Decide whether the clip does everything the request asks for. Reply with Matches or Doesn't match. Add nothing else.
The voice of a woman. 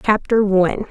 Matches